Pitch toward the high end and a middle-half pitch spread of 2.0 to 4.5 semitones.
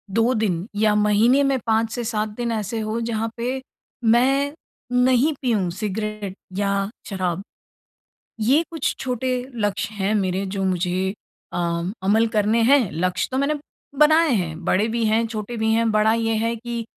Yes: high, 220 Hz; average, 3.1 semitones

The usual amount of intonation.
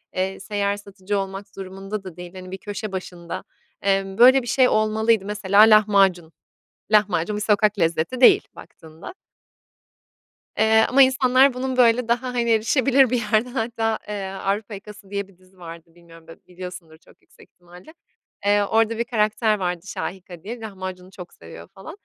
Yes: average, 3.3 semitones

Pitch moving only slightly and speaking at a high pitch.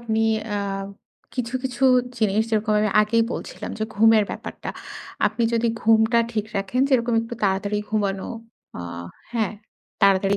Yes: narrow, 2.3 semitones; high, 220 Hz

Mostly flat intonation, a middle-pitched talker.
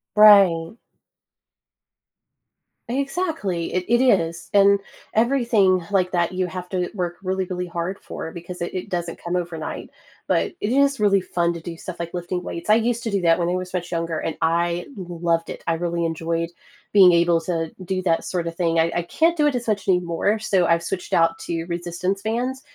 No: average, 3.0 semitones; medium, 180 Hz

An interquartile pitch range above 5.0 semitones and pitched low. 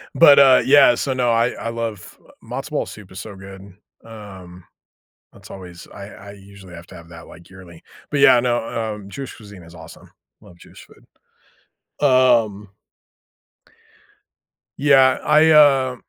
Yes: wide, 5.5 semitones; low, 105 Hz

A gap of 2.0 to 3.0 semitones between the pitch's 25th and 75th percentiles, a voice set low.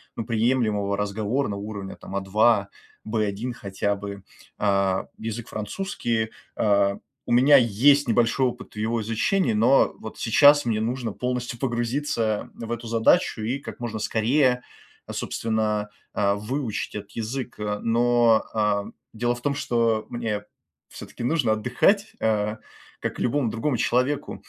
Yes: average, 2.7 semitones; low, 115 Hz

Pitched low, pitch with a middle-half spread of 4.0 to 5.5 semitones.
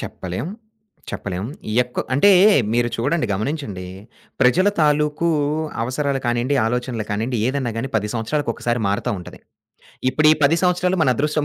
Yes: low, 125 Hz; average, 4.7 semitones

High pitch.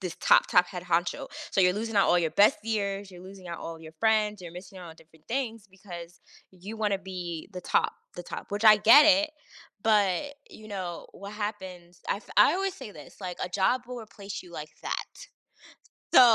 Yes: high, 195 Hz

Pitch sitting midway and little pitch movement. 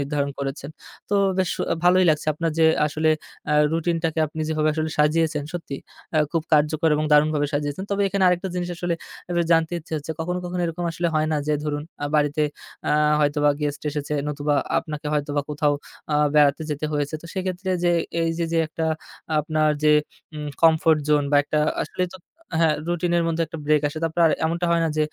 Yes: medium, 155 Hz; narrow, 2.1 semitones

